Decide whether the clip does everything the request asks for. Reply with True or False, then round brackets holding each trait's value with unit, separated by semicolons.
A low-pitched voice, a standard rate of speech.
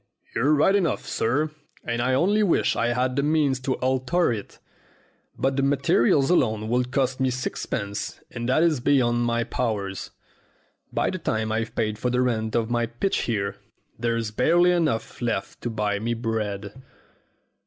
True (125 Hz; 165 wpm)